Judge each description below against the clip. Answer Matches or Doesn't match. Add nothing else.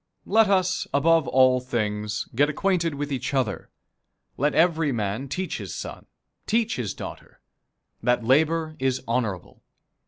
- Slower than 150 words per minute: Matches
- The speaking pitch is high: Doesn't match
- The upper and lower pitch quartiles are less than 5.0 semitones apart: Doesn't match